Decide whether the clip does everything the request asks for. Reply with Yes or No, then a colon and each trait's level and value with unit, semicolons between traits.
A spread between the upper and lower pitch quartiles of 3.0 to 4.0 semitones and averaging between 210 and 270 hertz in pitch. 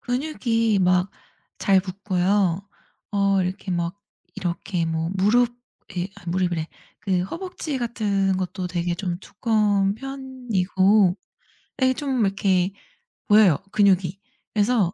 No: average, 3.7 semitones; high, 195 Hz